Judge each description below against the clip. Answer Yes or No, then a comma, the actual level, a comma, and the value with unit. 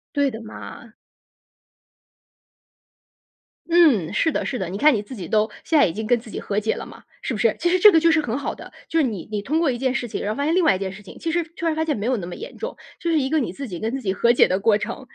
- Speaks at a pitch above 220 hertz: Yes, high, 240 Hz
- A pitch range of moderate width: No, wide, 7.0 semitones